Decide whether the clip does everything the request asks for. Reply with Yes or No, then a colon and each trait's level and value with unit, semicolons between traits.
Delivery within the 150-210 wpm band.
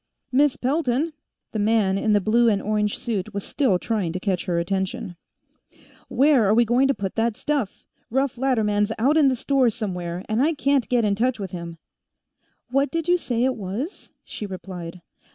Yes: average, 190 wpm